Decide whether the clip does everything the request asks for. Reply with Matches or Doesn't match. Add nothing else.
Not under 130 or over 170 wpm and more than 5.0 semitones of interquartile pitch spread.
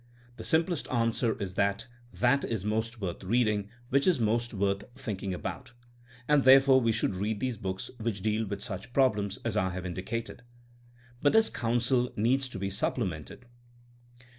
Doesn't match